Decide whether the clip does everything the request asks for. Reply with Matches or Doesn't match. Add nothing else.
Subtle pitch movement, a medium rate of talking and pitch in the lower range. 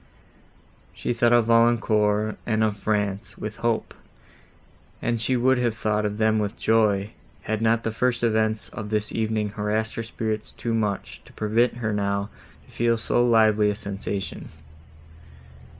Matches